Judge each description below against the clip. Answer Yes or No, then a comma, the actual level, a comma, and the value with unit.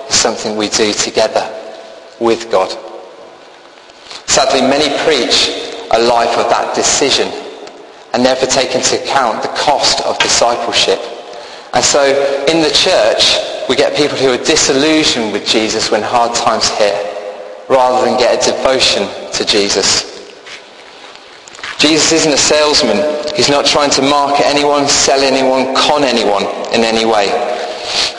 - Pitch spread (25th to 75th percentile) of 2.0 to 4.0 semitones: Yes, average, 3.4 semitones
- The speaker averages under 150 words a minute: Yes, average, 140 wpm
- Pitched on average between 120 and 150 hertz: Yes, low, 135 Hz